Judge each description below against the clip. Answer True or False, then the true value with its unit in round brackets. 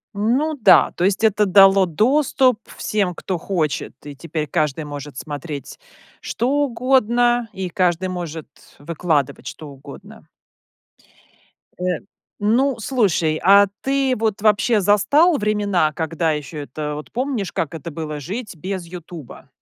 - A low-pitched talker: False (185 Hz)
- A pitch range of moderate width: False (6.0 semitones)